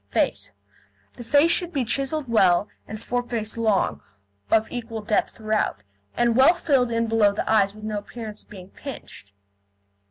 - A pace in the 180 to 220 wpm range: No, average, 160 wpm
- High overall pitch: Yes, high, 225 Hz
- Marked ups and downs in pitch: No, average, 2.7 semitones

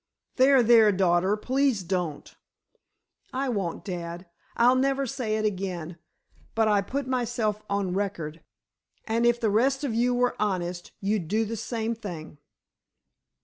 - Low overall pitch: No, high, 215 Hz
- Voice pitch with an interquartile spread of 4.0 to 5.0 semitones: Yes, average, 4.7 semitones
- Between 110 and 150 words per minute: Yes, average, 145 wpm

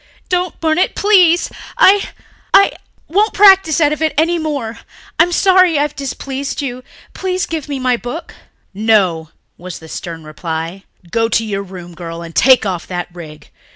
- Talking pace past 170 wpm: No, average, 165 wpm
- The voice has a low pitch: No, very high, 260 Hz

